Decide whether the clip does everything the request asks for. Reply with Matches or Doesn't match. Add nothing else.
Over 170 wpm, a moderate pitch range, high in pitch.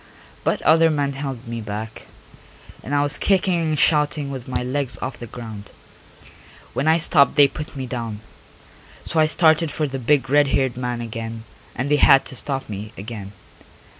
Doesn't match